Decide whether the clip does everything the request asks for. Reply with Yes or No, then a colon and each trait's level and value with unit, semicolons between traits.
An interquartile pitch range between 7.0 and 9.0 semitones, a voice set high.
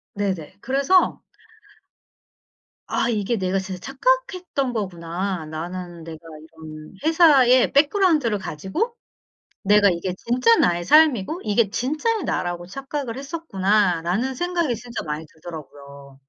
Yes: wide, 8.1 semitones; high, 205 Hz